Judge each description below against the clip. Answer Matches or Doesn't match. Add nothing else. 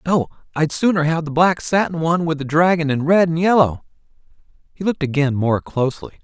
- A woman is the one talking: Doesn't match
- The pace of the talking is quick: Doesn't match